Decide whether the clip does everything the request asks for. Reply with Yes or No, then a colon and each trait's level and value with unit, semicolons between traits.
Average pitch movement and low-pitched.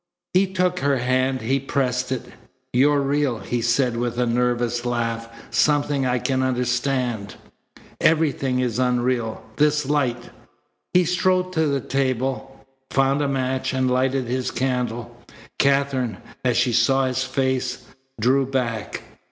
No: narrow, 2.1 semitones; low, 130 Hz